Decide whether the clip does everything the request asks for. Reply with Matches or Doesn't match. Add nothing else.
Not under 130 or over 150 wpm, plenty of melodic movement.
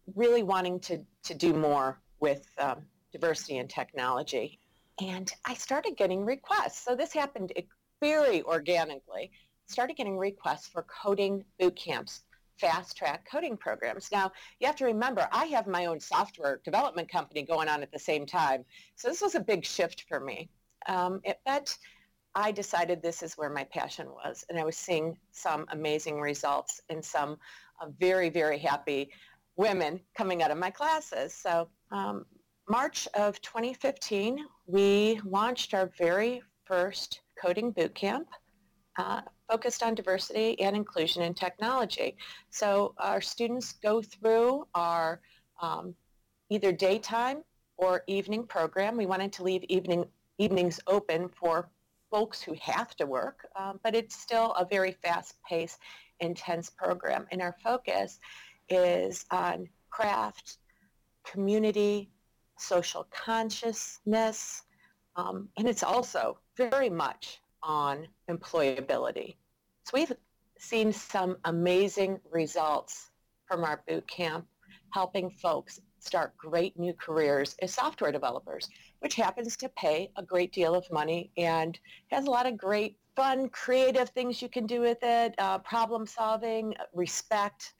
Doesn't match